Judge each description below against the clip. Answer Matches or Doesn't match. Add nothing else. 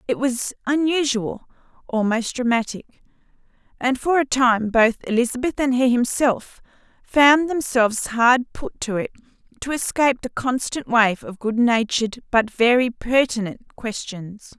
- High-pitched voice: Matches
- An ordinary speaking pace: Doesn't match